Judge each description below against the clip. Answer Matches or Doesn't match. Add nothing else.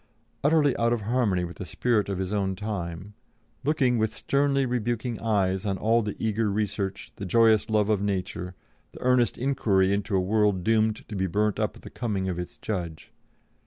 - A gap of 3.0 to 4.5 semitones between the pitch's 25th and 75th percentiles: Matches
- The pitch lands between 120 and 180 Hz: Doesn't match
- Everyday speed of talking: Matches